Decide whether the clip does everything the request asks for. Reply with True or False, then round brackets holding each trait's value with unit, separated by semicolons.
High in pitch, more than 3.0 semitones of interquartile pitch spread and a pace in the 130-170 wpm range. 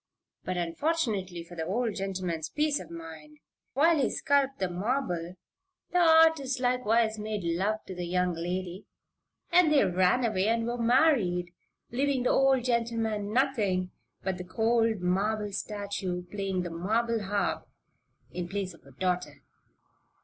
True (205 Hz; 5.4 semitones; 145 wpm)